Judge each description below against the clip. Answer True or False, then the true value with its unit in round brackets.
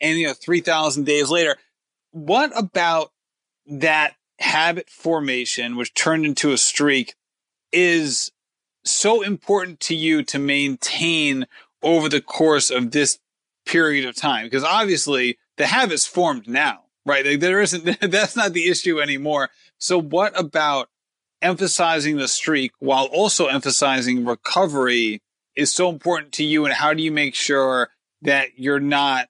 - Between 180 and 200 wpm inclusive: False (145 wpm)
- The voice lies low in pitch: False (150 Hz)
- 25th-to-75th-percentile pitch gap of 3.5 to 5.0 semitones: True (3.8 semitones)